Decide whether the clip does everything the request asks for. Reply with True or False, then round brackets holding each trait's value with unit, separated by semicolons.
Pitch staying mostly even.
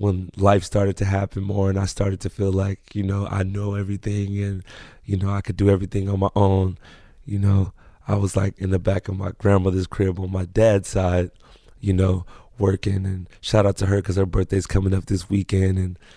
True (1.0 semitones)